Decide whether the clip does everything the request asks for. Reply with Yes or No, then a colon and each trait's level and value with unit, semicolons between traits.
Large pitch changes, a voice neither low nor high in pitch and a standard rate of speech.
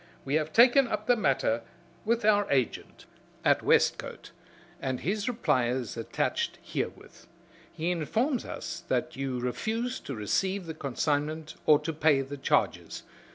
Yes: wide, 7.9 semitones; medium, 155 Hz; average, 145 wpm